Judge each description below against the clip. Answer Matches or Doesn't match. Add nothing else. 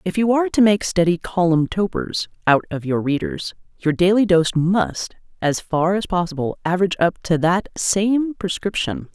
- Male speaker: Doesn't match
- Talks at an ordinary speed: Matches